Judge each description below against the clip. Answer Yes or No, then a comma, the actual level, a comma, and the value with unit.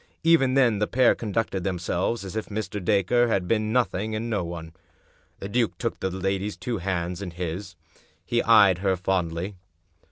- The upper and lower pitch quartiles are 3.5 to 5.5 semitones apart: Yes, average, 3.9 semitones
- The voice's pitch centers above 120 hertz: No, low, 100 Hz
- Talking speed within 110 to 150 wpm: No, average, 170 wpm